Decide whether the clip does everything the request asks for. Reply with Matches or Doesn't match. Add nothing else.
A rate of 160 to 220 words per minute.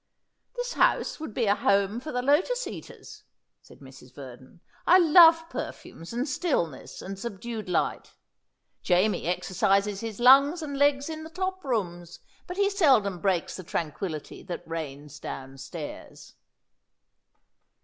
Doesn't match